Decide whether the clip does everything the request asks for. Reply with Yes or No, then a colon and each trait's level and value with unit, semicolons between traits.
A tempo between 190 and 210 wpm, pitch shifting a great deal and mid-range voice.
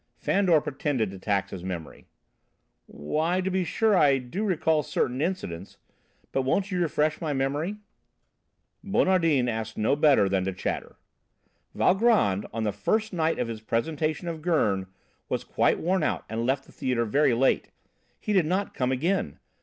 No: average, 160 wpm; wide, 8.0 semitones; medium, 145 Hz